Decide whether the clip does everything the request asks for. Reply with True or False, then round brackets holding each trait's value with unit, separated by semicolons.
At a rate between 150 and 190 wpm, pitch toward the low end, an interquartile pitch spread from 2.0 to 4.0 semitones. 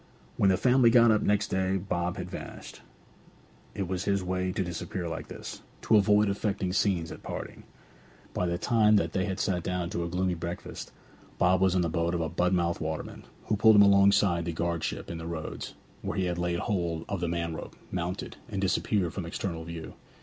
False (200 wpm; 90 Hz; 2.6 semitones)